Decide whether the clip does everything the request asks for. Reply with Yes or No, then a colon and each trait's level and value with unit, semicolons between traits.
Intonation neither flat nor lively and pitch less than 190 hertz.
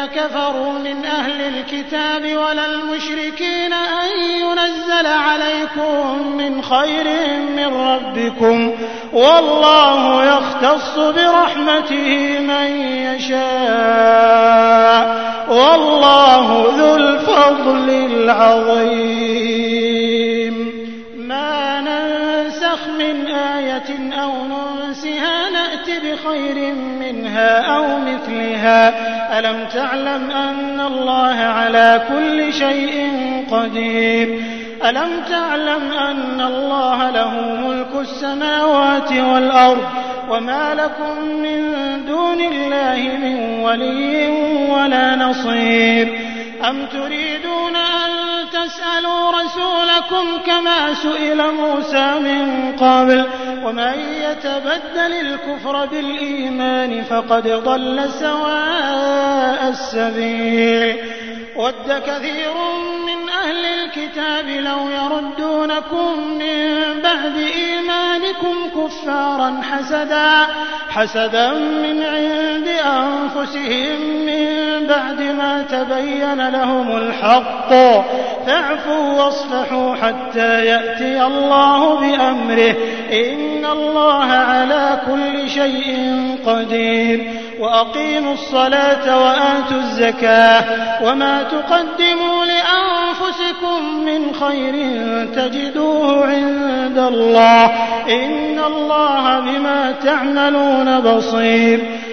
No: average, 3.2 semitones; very high, 280 Hz